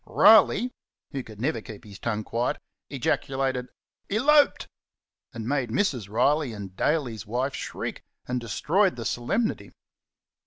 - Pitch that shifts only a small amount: No, wide, 5.4 semitones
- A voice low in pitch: Yes, low, 125 Hz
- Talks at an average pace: No, slow, 125 wpm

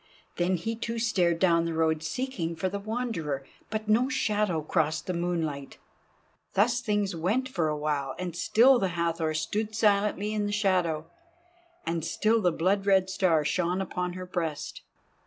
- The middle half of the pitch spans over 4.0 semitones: Yes, average, 4.4 semitones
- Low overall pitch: No, medium, 185 Hz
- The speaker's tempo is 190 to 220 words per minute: No, average, 160 wpm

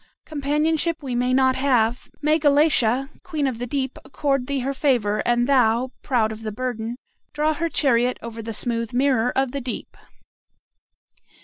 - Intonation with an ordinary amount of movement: Yes, average, 3.1 semitones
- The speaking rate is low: No, average, 165 wpm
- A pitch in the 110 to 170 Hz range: No, very high, 260 Hz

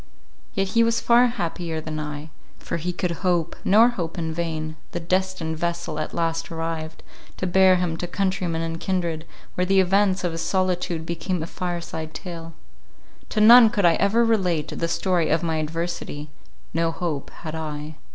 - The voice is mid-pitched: Yes, medium, 170 Hz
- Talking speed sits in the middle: Yes, average, 175 wpm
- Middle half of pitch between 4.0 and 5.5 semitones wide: No, narrow, 2.6 semitones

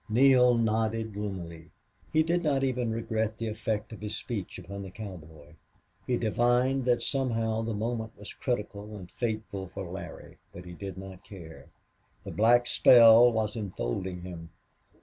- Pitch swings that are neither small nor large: Yes, average, 3.8 semitones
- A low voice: Yes, low, 110 Hz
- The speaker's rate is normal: Yes, average, 160 wpm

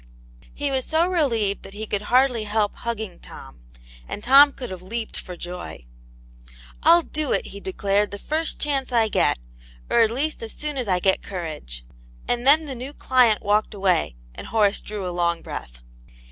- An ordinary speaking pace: Yes, average, 185 wpm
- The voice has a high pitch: Yes, high, 220 Hz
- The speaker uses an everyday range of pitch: No, wide, 5.7 semitones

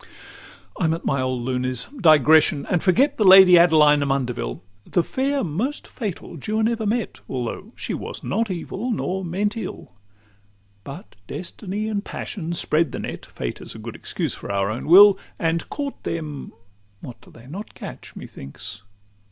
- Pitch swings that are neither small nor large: No, wide, 7.2 semitones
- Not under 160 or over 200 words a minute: Yes, average, 165 wpm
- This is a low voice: No, medium, 170 Hz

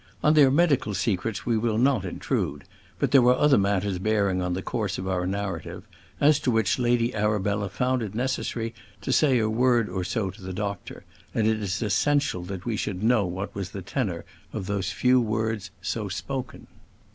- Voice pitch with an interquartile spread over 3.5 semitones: Yes, average, 4.1 semitones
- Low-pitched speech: Yes, low, 110 Hz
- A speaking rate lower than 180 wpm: No, average, 195 wpm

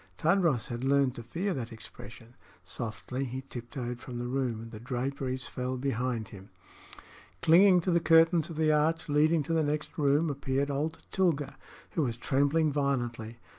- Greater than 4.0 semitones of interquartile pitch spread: Yes, average, 4.5 semitones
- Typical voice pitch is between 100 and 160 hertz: Yes, low, 135 Hz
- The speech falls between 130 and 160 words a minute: No, average, 170 wpm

